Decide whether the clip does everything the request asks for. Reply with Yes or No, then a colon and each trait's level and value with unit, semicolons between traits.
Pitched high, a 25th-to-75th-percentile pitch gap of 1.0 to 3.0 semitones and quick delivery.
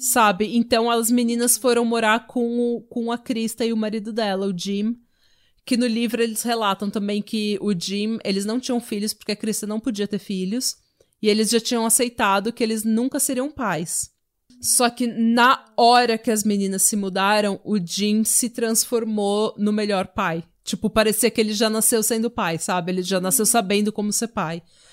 Yes: high, 220 Hz; narrow, 2.4 semitones; fast, 190 wpm